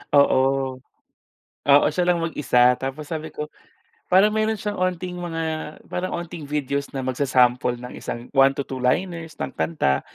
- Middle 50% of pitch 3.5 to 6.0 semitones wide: Yes, average, 5.0 semitones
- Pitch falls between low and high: Yes, medium, 150 Hz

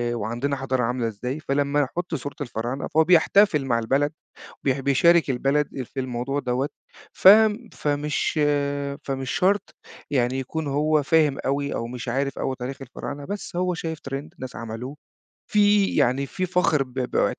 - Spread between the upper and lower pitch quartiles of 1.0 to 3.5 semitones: Yes, average, 3.2 semitones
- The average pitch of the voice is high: No, medium, 140 Hz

